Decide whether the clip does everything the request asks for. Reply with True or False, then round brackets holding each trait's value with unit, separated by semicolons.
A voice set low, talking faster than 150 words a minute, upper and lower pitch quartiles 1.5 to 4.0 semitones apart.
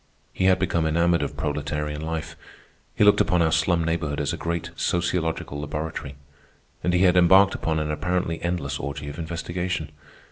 True (80 Hz; 170 wpm; 2.8 semitones)